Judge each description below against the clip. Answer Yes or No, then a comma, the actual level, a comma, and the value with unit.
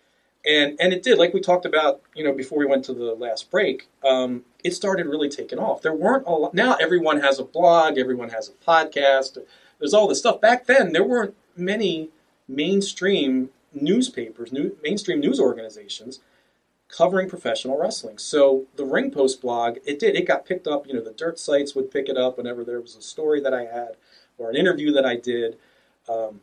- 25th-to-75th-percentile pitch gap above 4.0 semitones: Yes, average, 5.3 semitones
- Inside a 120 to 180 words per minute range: No, average, 200 wpm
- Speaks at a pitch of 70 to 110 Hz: No, medium, 140 Hz